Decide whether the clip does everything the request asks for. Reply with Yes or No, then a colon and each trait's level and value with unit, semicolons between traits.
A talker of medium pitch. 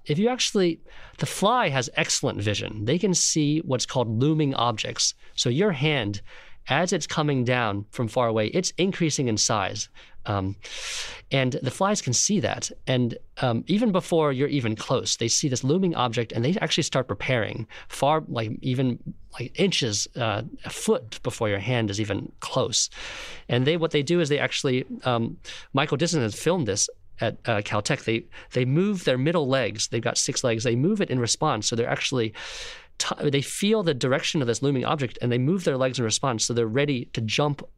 No: low, 130 Hz